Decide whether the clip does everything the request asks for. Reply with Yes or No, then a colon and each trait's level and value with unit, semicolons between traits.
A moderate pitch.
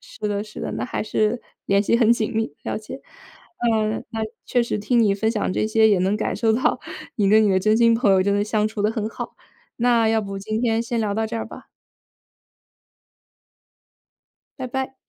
No: high, 220 Hz